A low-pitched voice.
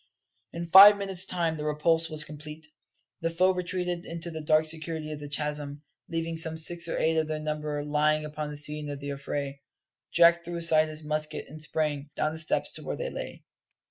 No: medium, 155 Hz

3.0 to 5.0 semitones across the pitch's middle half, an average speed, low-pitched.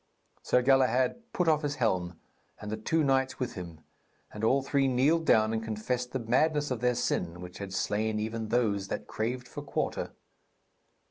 Yes: average, 3.9 semitones; average, 180 wpm; low, 125 Hz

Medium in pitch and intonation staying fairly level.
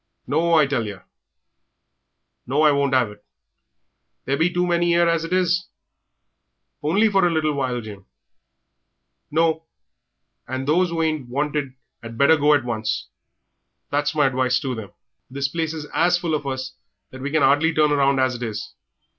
No: medium, 145 Hz; average, 3.9 semitones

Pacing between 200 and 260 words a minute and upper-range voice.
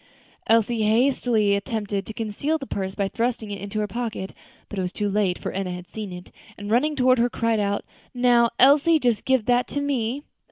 Yes: fast, 205 wpm; high, 225 Hz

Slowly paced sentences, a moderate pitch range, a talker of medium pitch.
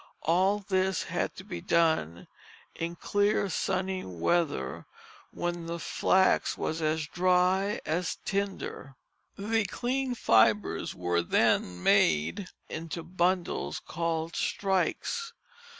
Yes: slow, 105 wpm; average, 3.5 semitones; medium, 175 Hz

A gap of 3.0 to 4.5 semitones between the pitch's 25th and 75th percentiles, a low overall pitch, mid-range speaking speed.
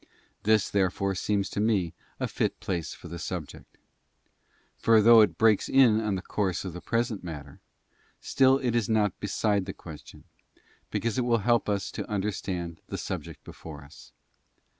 Yes: average, 3.8 semitones; low, 100 Hz; average, 170 wpm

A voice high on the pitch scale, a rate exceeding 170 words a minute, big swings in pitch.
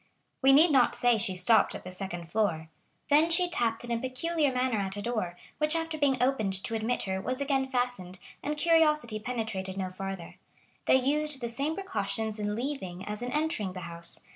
Yes: high, 240 Hz; average, 195 wpm; wide, 6.7 semitones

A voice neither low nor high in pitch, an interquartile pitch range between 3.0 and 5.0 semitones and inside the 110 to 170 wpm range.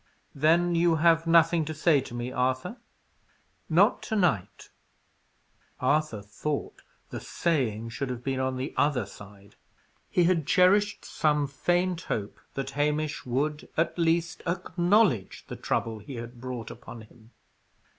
No: medium, 150 Hz; wide, 5.5 semitones; average, 140 wpm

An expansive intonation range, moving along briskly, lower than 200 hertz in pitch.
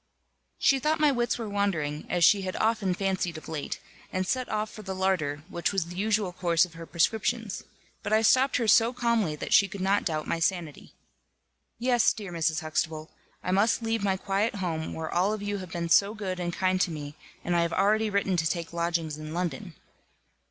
No: average, 4.1 semitones; fast, 210 wpm; medium, 185 Hz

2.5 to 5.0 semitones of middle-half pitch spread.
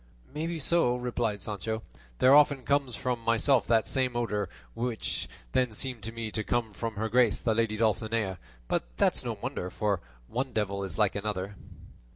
Yes: average, 2.9 semitones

